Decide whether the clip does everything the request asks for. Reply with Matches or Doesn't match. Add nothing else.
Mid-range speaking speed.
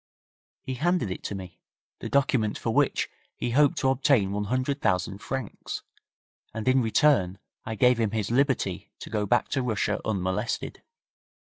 Matches